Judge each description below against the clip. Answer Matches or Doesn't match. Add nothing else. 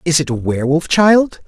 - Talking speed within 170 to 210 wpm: Matches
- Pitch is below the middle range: Doesn't match